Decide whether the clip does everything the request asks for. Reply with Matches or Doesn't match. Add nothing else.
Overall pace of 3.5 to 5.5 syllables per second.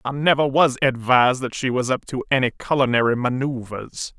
Matches